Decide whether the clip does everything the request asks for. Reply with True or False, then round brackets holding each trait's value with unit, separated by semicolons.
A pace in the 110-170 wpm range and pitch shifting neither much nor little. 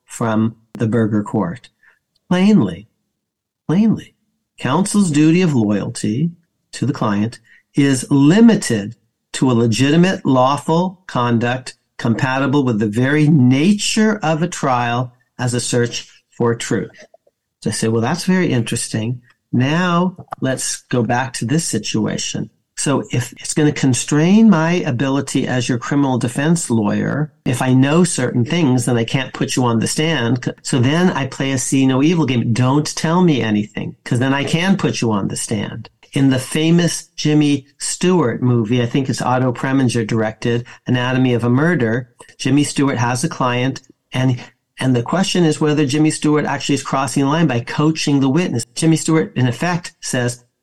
True (165 wpm; 4.4 semitones)